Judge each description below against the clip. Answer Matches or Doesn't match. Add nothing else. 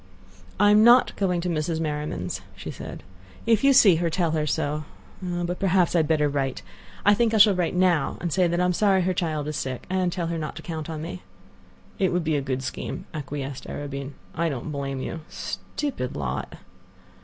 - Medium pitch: Matches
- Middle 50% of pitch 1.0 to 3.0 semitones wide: Doesn't match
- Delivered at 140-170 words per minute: Doesn't match